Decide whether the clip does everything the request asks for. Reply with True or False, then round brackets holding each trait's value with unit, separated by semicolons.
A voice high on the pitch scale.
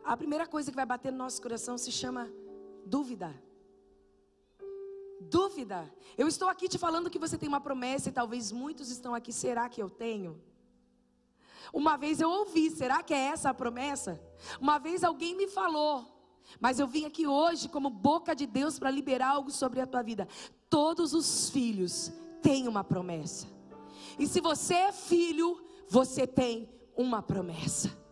True (270 Hz)